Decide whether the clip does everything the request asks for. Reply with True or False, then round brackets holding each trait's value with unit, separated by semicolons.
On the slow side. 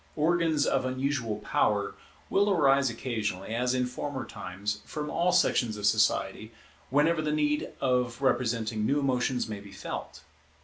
False (145 wpm)